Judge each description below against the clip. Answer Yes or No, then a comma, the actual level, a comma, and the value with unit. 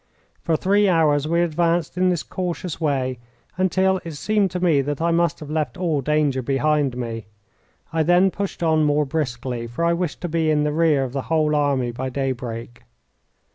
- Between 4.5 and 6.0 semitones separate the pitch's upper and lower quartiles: No, average, 3.9 semitones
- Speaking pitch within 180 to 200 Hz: No, medium, 155 Hz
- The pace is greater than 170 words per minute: Yes, average, 190 wpm